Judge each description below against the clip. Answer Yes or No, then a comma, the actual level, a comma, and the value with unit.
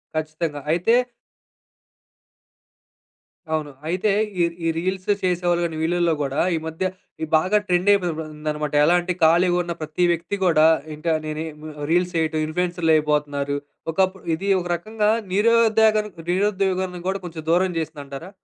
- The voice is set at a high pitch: No, medium, 175 Hz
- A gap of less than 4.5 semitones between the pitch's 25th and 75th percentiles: Yes, average, 3.1 semitones